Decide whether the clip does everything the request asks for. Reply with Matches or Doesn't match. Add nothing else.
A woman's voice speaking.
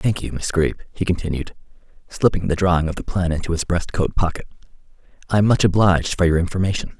Doesn't match